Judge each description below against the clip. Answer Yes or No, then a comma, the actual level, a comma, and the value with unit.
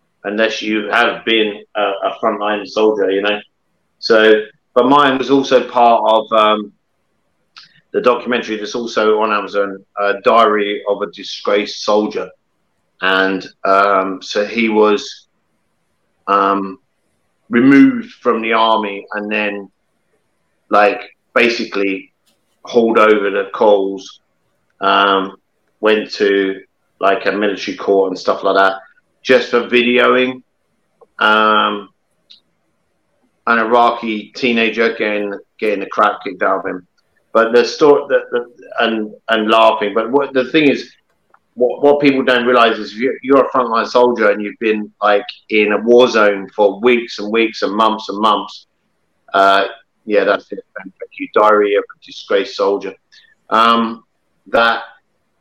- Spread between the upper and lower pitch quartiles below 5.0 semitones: Yes, average, 3.1 semitones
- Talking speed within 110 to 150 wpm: Yes, average, 140 wpm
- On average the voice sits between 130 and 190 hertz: No, low, 110 Hz